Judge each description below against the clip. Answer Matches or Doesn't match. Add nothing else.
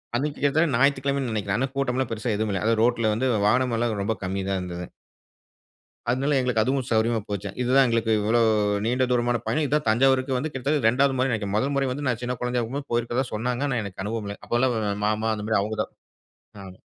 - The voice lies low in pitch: Matches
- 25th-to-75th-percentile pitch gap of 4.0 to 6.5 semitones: Doesn't match